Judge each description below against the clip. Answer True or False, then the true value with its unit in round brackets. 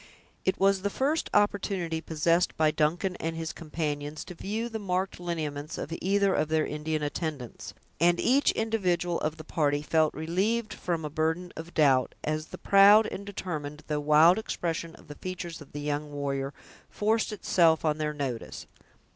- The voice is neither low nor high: True (165 Hz)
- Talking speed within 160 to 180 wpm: True (170 wpm)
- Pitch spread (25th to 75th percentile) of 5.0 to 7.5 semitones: False (3.8 semitones)